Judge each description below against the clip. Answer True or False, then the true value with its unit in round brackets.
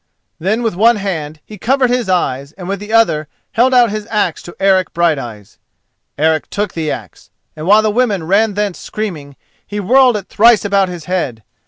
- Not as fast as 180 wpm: False (190 wpm)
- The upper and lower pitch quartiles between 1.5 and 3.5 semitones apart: False (5.0 semitones)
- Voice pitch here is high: True (195 Hz)